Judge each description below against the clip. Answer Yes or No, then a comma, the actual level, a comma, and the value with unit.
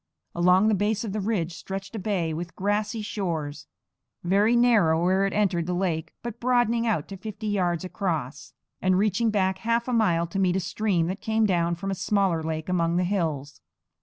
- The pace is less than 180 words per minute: No, average, 195 wpm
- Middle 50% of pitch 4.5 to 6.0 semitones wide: No, average, 3.7 semitones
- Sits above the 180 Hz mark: Yes, high, 190 Hz